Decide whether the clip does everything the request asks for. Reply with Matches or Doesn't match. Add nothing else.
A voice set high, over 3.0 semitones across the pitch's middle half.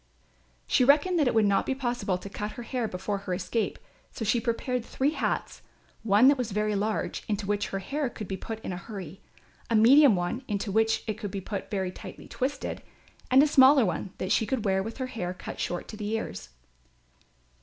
Matches